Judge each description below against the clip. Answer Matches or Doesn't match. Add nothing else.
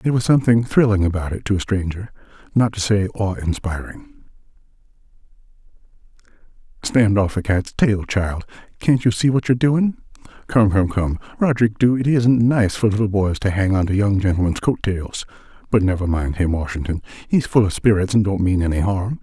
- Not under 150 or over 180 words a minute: Matches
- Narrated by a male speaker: Matches